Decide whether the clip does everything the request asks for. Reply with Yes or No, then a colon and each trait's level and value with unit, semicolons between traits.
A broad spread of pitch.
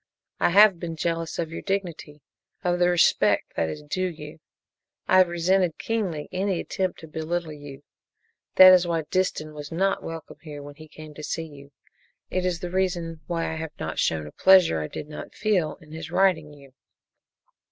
No: average, 3.3 semitones